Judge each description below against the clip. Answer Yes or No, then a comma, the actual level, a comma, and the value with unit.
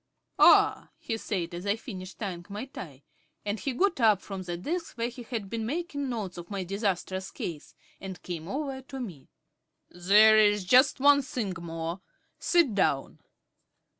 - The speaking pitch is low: No, high, 205 Hz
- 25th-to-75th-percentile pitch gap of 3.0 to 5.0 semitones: No, wide, 5.6 semitones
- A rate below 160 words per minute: No, average, 165 wpm